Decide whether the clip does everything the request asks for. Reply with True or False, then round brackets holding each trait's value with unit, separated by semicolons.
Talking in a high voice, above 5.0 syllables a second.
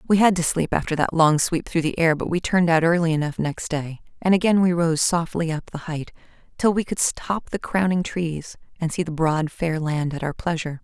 False (165 Hz; 5.3 syllables/s)